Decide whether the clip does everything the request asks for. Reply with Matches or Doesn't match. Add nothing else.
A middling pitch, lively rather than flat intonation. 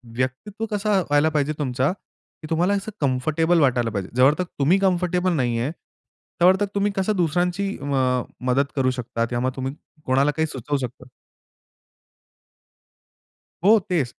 Matches